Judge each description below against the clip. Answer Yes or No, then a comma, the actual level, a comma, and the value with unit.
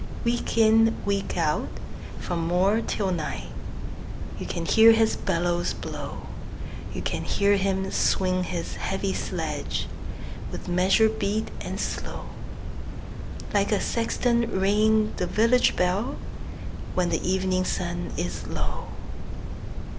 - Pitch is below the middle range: No, high, 190 Hz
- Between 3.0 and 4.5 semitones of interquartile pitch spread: Yes, average, 3.6 semitones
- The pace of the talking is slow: Yes, slow, 120 wpm